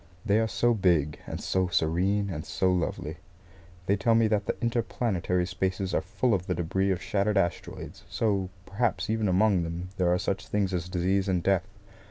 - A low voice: Yes, very low, 95 Hz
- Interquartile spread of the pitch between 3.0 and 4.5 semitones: No, narrow, 2.4 semitones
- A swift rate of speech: No, average, 190 wpm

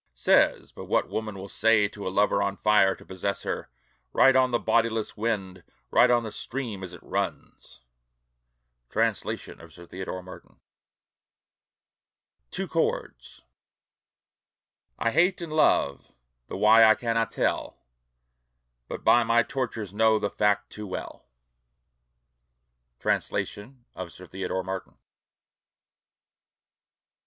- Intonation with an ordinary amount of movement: Yes, average, 3.5 semitones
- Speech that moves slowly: Yes, slow, 125 wpm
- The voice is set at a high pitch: No, low, 105 Hz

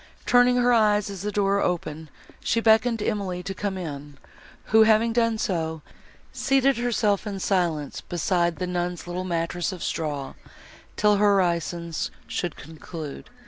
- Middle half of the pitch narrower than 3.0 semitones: No, average, 4.2 semitones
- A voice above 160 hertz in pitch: Yes, medium, 185 Hz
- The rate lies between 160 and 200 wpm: No, average, 150 wpm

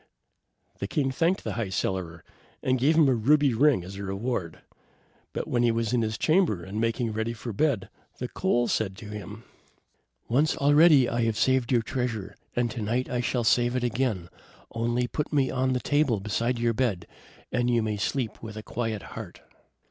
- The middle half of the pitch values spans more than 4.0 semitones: No, average, 3.2 semitones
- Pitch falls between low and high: No, low, 120 Hz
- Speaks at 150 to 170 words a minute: No, average, 195 wpm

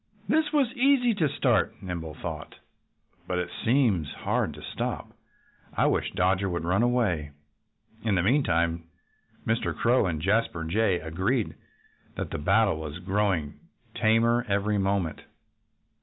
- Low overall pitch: Yes, low, 100 Hz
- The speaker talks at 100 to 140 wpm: Yes, slow, 135 wpm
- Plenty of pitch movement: Yes, wide, 5.7 semitones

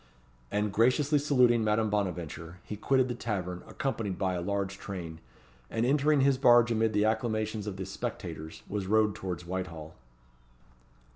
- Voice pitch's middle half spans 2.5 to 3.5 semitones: No, average, 4.2 semitones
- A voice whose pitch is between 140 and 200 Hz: No, low, 105 Hz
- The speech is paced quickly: No, average, 150 wpm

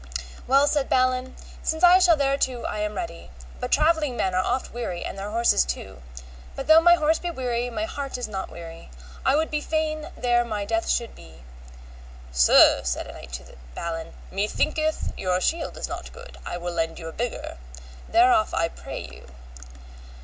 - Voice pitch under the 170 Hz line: No, high, 245 Hz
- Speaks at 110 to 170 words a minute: No, average, 185 wpm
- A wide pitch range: Yes, wide, 9.0 semitones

